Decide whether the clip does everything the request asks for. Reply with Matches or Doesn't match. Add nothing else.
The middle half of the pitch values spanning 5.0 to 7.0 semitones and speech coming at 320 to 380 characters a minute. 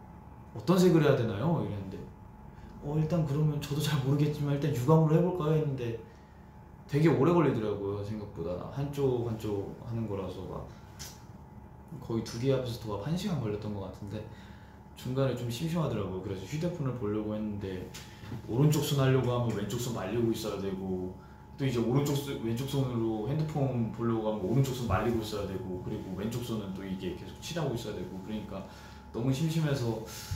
Matches